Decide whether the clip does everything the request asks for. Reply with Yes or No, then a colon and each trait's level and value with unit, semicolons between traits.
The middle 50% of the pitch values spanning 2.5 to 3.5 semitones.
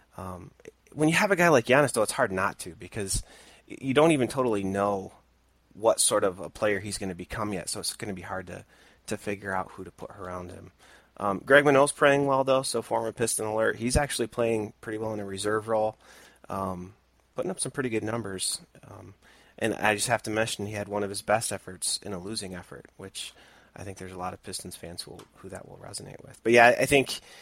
No: average, 4.0 semitones